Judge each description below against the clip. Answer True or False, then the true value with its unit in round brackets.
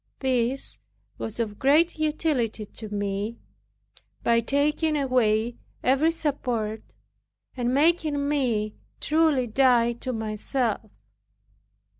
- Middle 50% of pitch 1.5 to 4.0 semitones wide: False (4.6 semitones)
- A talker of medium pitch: False (250 Hz)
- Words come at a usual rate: False (95 wpm)